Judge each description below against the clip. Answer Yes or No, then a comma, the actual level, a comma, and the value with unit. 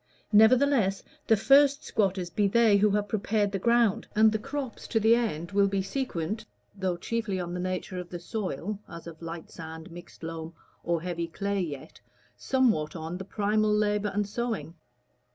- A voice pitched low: No, high, 200 Hz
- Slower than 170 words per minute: No, average, 175 wpm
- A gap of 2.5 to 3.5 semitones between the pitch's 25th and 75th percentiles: No, average, 4.2 semitones